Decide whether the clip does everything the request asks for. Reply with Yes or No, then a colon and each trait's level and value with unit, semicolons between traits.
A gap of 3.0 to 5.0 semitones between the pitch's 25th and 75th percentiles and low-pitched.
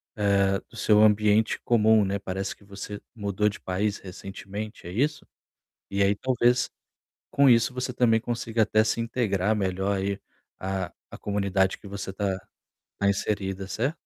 No: narrow, 2.4 semitones; low, 105 Hz